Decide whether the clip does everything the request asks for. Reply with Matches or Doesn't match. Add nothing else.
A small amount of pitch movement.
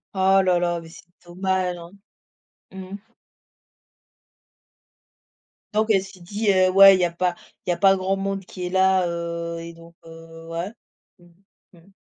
Matches